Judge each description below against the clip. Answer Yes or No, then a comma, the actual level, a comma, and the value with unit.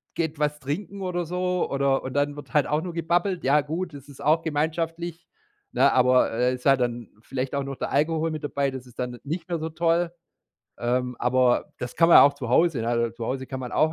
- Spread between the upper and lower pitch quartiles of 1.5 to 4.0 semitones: No, average, 4.4 semitones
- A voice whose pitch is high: No, medium, 145 Hz